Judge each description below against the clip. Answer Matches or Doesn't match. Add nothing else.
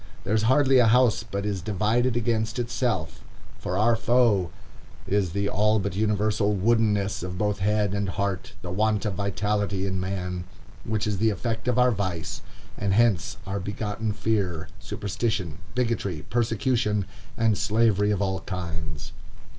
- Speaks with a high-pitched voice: Doesn't match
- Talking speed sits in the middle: Matches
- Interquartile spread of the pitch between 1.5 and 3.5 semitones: Matches